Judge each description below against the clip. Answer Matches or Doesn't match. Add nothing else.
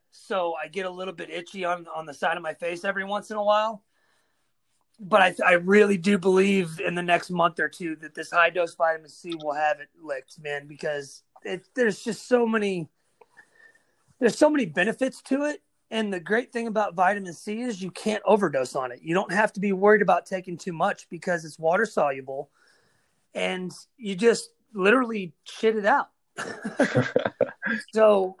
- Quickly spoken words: Doesn't match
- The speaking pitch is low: Doesn't match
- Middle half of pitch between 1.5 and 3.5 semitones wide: Doesn't match